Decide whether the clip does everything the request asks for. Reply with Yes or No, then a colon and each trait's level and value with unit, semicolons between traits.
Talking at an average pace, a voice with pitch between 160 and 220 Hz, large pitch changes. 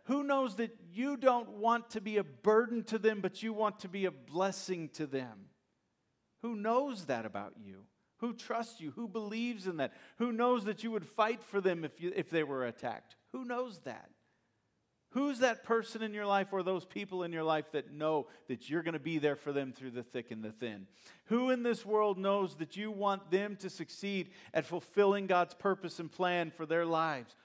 No: fast, 215 wpm; high, 190 Hz; wide, 6.1 semitones